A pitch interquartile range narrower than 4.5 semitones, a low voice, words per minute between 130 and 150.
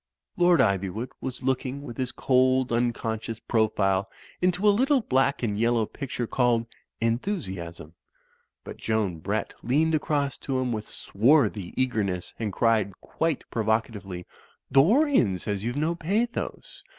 No: average, 4.9 semitones; low, 120 Hz; average, 140 wpm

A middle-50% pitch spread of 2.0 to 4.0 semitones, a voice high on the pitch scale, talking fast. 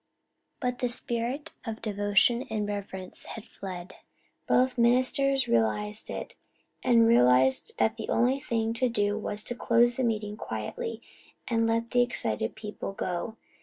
No: average, 2.9 semitones; high, 225 Hz; average, 145 wpm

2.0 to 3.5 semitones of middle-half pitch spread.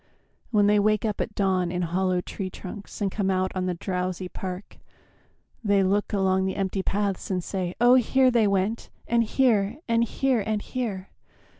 Yes: narrow, 2.6 semitones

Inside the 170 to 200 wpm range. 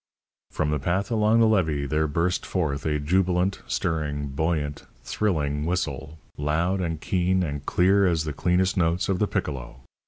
No: average, 160 wpm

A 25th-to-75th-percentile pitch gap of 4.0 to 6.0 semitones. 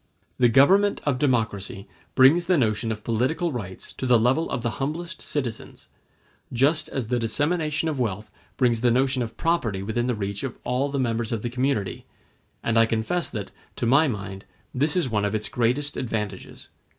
Yes: average, 4.4 semitones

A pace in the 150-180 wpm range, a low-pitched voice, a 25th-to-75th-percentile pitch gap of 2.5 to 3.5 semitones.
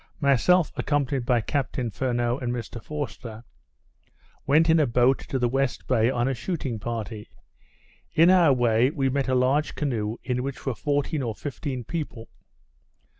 Yes: average, 160 wpm; low, 130 Hz; average, 3.2 semitones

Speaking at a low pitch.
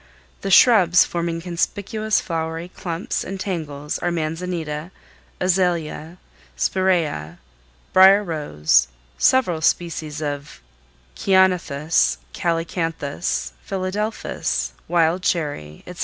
No: medium, 170 Hz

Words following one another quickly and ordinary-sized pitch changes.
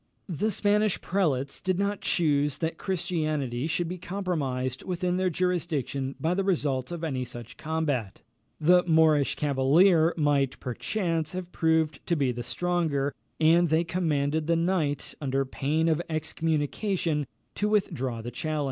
No: average, 145 wpm; average, 4.0 semitones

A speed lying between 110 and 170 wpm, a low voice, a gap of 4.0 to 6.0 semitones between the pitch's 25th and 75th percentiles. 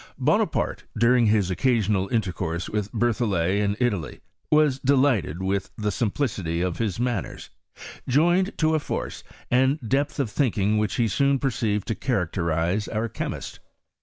Yes: average, 150 wpm; low, 110 Hz; average, 5.1 semitones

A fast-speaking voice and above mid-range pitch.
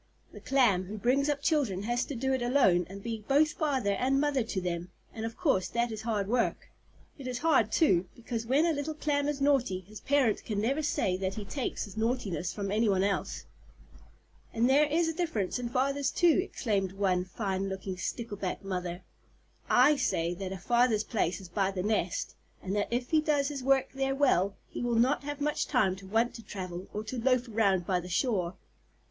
Yes: fast, 210 wpm; high, 230 Hz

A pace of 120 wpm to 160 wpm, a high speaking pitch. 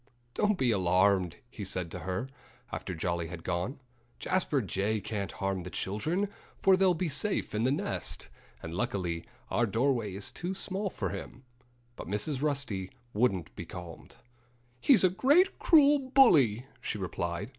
No: average, 155 wpm; low, 105 Hz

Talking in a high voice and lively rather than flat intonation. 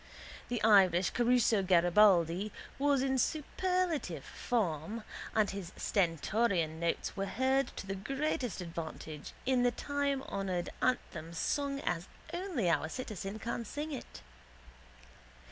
Yes: high, 215 Hz; wide, 7.0 semitones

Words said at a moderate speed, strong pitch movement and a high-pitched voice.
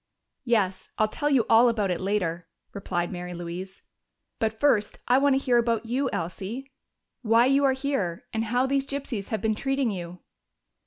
Yes: average, 175 wpm; wide, 5.8 semitones; high, 225 Hz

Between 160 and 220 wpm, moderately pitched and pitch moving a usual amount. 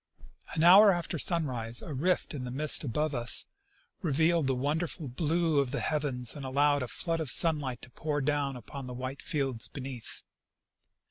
Yes: average, 175 wpm; medium, 145 Hz; average, 3.7 semitones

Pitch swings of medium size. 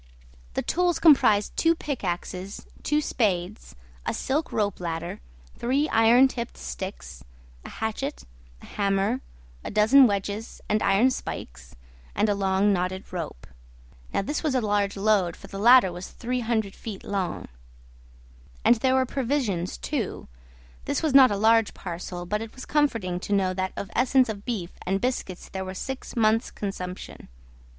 Yes: average, 5.0 semitones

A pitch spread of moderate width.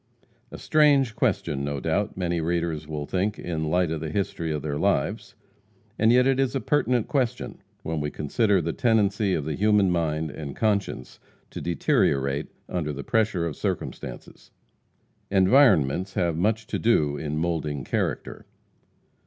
No: wide, 5.9 semitones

